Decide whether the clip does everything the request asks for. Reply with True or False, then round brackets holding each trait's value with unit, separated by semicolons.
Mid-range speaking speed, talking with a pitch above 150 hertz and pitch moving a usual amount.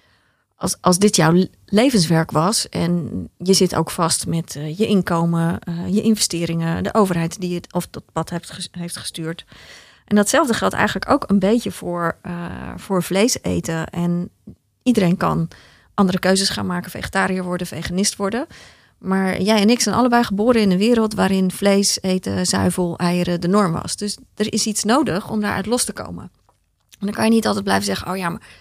True (190 wpm; 185 Hz; 3.4 semitones)